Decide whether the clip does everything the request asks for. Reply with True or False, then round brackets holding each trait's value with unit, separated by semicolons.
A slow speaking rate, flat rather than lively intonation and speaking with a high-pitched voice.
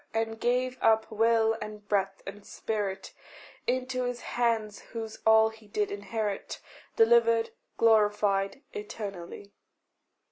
True (110 wpm; 1.9 semitones; 220 Hz)